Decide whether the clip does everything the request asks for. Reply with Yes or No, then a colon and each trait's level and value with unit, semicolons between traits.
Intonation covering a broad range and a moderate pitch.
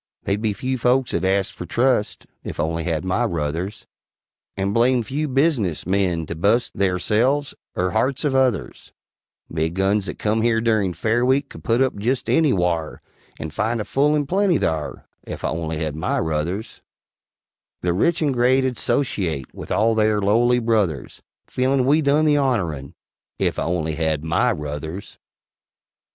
No: wide, 7.1 semitones; low, 105 Hz